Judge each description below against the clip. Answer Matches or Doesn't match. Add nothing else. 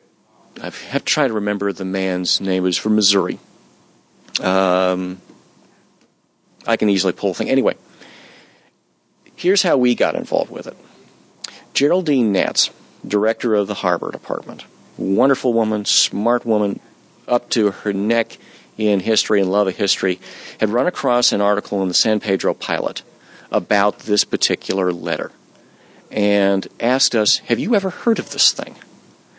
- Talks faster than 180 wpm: Doesn't match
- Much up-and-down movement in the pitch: Doesn't match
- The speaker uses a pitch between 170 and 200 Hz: Doesn't match